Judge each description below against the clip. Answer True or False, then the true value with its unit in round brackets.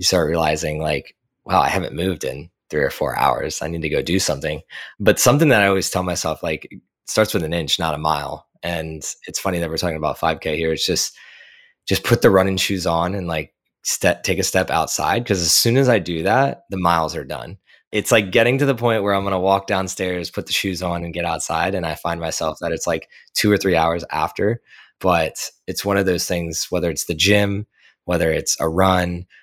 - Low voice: True (90 Hz)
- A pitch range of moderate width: True (3.1 semitones)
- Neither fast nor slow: False (235 wpm)